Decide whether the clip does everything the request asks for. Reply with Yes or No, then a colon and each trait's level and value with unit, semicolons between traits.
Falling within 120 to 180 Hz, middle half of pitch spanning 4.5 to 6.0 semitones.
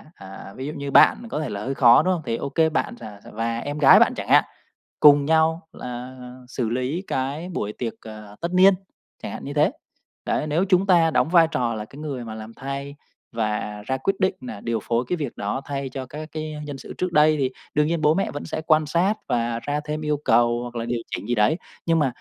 Yes: medium, 140 Hz; average, 4.9 semitones